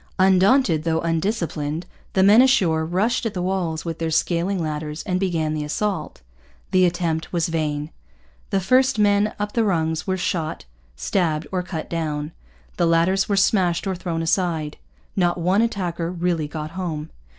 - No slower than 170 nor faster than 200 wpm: No, average, 160 wpm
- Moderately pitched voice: Yes, medium, 175 Hz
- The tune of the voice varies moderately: Yes, average, 3.1 semitones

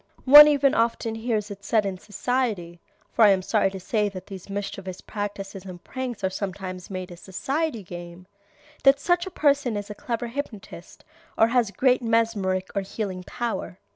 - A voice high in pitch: Yes, high, 205 Hz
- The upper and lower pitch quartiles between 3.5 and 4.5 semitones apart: Yes, average, 4.2 semitones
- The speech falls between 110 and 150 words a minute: No, average, 175 wpm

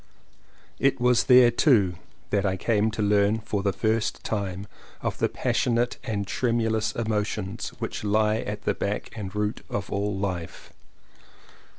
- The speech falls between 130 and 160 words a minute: Yes, average, 155 wpm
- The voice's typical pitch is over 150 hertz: No, low, 105 Hz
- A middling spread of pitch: No, narrow, 2.1 semitones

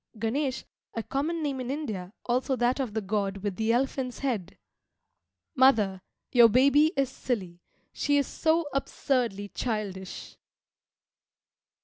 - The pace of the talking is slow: Yes, slow, 125 wpm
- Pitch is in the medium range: No, high, 245 Hz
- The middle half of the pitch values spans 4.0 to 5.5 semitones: Yes, average, 4.8 semitones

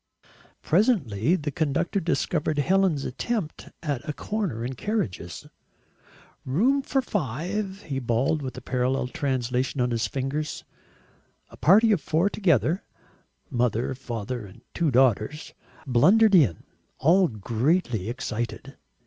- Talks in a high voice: No, medium, 140 Hz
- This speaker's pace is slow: Yes, slow, 120 wpm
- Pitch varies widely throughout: Yes, wide, 6.7 semitones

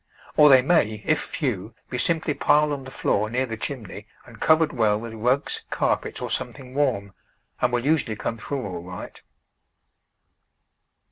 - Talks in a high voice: No, low, 125 Hz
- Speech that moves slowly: No, average, 160 wpm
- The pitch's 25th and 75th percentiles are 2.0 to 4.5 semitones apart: No, average, 5.0 semitones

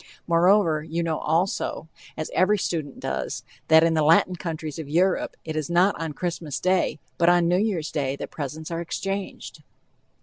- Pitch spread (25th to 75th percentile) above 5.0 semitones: No, narrow, 2.4 semitones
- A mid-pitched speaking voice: Yes, medium, 165 Hz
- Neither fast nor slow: Yes, average, 175 wpm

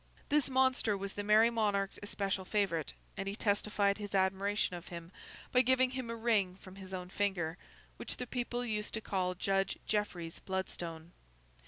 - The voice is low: No, high, 200 Hz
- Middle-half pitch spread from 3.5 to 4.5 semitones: No, average, 2.8 semitones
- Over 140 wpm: Yes, average, 170 wpm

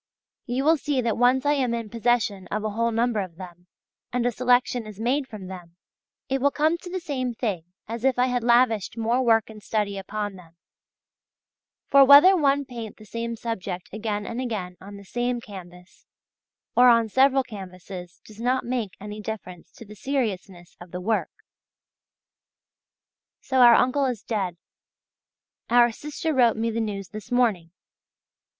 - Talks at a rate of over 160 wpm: Yes, average, 170 wpm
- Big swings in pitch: No, average, 3.9 semitones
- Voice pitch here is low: No, high, 230 Hz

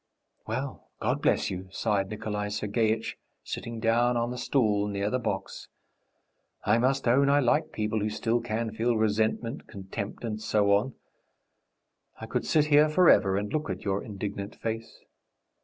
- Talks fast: No, average, 155 wpm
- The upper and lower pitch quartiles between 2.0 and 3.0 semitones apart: Yes, average, 2.7 semitones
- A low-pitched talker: Yes, low, 110 Hz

